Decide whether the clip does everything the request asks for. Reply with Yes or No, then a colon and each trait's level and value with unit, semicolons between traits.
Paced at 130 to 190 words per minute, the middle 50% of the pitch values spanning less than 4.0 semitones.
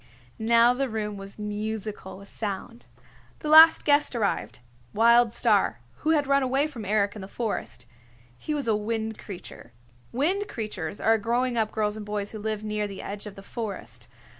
Yes: average, 180 wpm; average, 2.8 semitones